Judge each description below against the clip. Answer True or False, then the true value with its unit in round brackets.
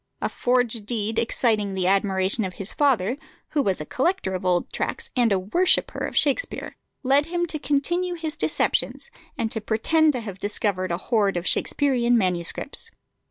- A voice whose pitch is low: False (225 Hz)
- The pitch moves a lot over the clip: True (6.5 semitones)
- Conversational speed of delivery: True (170 wpm)